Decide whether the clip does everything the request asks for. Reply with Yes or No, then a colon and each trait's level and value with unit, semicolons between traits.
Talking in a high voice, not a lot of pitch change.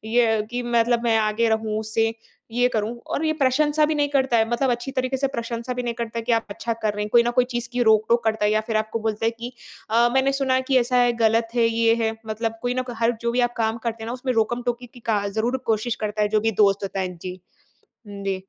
Yes: high, 230 Hz; narrow, 2.0 semitones